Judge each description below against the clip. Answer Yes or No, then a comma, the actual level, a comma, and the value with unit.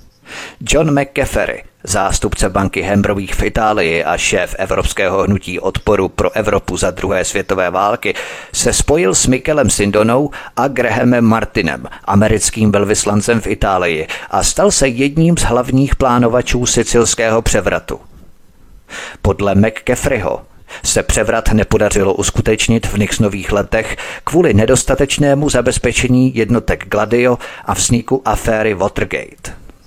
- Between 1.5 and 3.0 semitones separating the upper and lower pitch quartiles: No, average, 3.5 semitones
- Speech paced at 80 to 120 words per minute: Yes, slow, 115 wpm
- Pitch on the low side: Yes, low, 115 Hz